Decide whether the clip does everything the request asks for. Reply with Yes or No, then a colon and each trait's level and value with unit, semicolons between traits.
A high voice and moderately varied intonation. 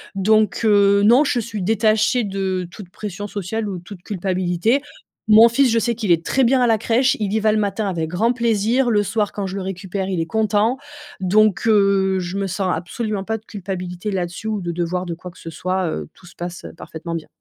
Yes: high, 200 Hz; average, 3.2 semitones